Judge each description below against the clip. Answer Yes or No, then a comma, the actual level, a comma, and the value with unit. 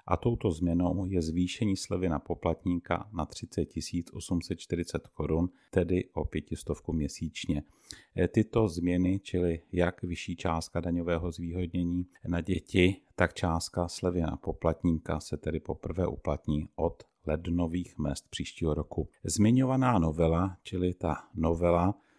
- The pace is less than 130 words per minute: Yes, average, 120 wpm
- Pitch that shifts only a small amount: Yes, narrow, 2.0 semitones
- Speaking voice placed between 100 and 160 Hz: No, very low, 90 Hz